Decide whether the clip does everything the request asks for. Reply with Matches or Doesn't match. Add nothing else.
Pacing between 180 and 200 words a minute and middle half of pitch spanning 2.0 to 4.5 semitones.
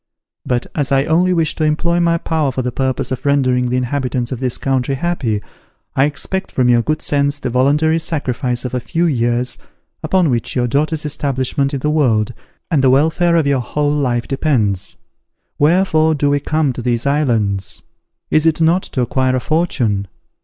Matches